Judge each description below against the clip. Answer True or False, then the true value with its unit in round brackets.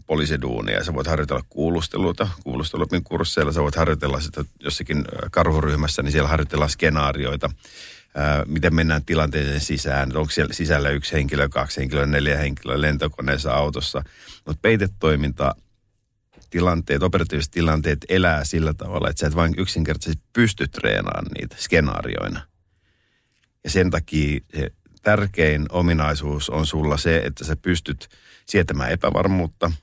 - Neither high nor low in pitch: False (75 Hz)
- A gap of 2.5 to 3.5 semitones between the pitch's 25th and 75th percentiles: True (2.8 semitones)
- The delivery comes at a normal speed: True (125 wpm)